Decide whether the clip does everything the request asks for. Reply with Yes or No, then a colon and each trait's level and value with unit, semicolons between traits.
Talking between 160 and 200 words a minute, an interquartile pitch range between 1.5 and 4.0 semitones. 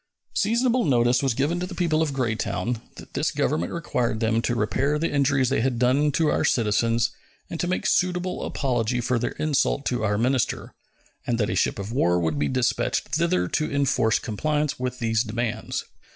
No: average, 190 wpm; average, 4.9 semitones